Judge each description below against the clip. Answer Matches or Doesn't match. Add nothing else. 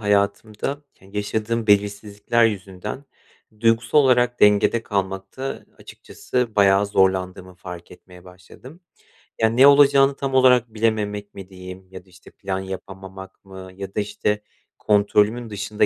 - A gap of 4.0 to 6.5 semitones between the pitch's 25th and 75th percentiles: Doesn't match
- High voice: Doesn't match